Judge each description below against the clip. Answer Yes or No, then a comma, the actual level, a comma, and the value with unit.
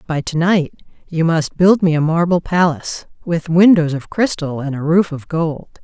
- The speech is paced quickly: No, average, 195 wpm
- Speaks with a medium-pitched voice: Yes, medium, 165 Hz